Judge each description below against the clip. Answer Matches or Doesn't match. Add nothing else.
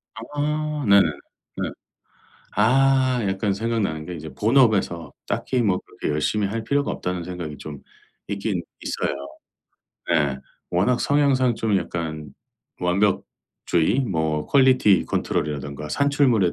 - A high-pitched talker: Doesn't match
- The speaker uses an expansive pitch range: Matches